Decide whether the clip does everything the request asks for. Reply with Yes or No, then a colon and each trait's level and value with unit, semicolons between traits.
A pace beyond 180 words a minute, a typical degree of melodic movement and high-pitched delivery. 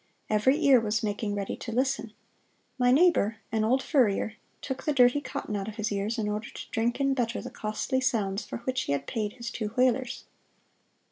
Yes: average, 200 wpm; average, 3.5 semitones; high, 230 Hz